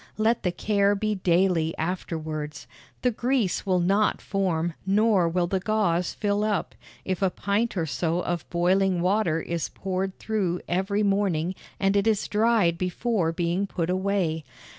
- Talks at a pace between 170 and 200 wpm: No, average, 155 wpm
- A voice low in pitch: No, high, 190 Hz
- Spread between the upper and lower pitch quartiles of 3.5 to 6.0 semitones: No, average, 3.0 semitones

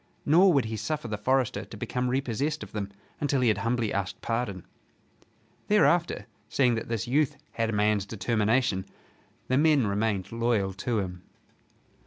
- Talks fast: No, average, 160 wpm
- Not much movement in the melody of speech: No, average, 4.3 semitones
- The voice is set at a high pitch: No, low, 115 Hz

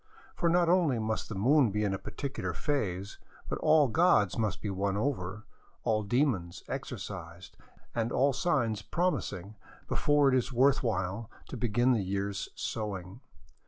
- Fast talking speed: No, average, 155 wpm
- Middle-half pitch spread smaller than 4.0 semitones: No, wide, 5.6 semitones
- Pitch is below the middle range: Yes, low, 110 Hz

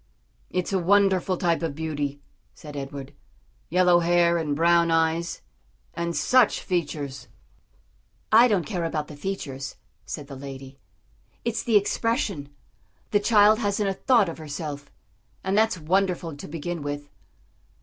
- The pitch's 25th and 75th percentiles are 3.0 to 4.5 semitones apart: No, average, 5.0 semitones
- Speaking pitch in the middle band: Yes, medium, 170 Hz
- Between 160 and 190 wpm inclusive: No, average, 140 wpm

